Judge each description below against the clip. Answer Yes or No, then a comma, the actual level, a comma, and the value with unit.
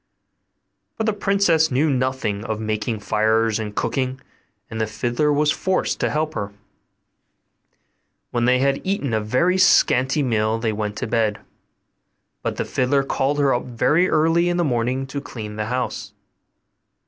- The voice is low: Yes, low, 130 Hz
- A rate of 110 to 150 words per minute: No, average, 160 wpm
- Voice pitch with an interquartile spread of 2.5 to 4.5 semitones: No, average, 5.3 semitones